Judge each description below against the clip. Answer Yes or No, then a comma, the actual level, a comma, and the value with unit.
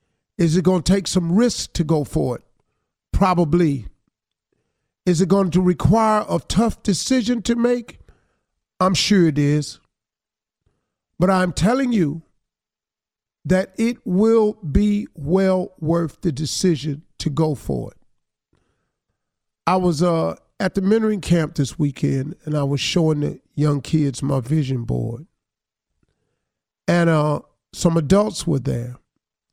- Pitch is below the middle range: No, medium, 170 Hz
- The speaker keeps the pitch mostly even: No, average, 4.5 semitones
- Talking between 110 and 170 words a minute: Yes, slow, 135 wpm